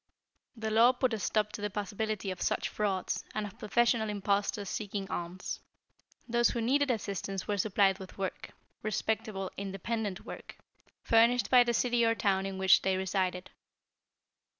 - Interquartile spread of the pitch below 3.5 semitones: Yes, average, 2.8 semitones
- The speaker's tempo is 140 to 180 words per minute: Yes, average, 155 wpm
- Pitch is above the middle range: Yes, high, 210 Hz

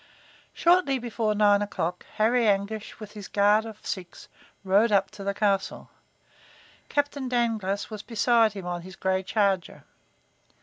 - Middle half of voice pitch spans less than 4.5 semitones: Yes, narrow, 2.6 semitones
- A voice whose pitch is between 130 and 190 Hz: No, high, 210 Hz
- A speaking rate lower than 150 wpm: Yes, average, 140 wpm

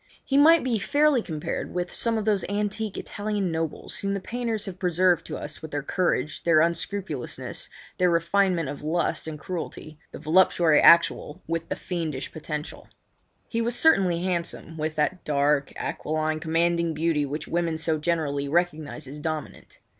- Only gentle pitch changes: No, average, 3.7 semitones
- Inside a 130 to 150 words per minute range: No, average, 160 wpm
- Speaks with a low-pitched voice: No, medium, 170 Hz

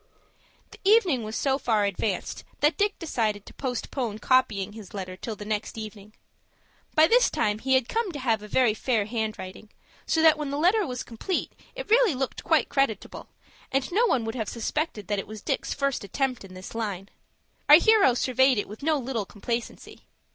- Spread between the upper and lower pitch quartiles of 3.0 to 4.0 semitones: No, wide, 5.6 semitones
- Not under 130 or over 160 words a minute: No, average, 190 wpm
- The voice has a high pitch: Yes, high, 240 Hz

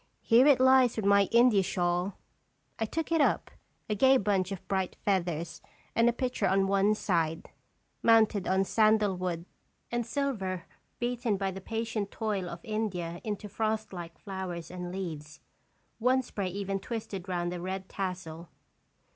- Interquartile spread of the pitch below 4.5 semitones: Yes, average, 3.7 semitones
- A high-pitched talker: Yes, high, 195 Hz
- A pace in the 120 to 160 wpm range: Yes, average, 155 wpm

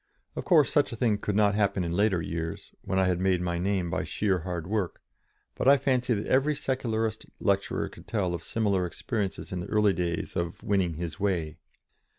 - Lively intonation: No, average, 3.9 semitones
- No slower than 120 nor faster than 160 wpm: No, average, 200 wpm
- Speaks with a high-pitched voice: No, low, 100 Hz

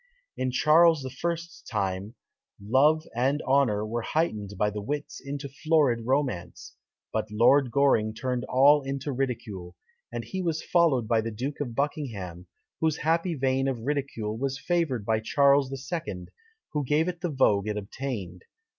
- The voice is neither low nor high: No, low, 130 Hz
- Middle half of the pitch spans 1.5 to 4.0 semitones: No, average, 5.2 semitones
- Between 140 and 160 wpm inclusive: Yes, average, 155 wpm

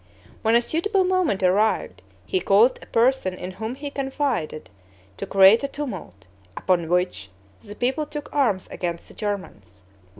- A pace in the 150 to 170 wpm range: Yes, average, 155 wpm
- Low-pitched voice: No, high, 210 Hz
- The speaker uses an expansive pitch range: Yes, wide, 7.1 semitones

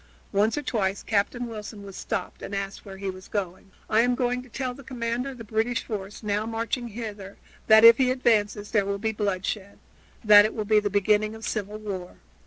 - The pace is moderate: No, fast, 210 wpm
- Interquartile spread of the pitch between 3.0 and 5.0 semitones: No, narrow, 2.5 semitones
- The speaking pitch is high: Yes, high, 215 Hz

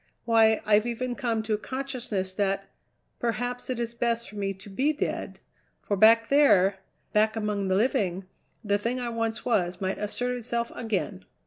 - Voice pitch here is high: Yes, high, 225 Hz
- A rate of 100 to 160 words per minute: No, average, 175 wpm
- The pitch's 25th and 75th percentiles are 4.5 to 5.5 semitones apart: No, average, 3.1 semitones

